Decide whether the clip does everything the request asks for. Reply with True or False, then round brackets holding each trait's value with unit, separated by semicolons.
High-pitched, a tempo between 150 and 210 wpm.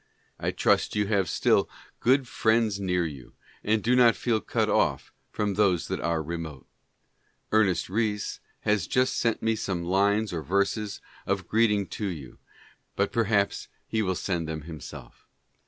False (100 Hz; 160 wpm)